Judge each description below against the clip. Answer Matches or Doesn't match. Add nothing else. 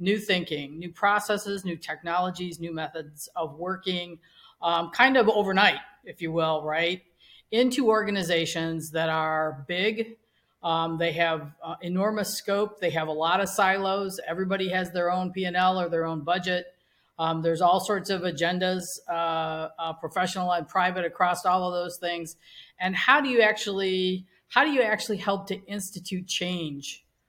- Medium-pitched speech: Matches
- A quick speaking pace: Doesn't match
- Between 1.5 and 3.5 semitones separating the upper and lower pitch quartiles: Matches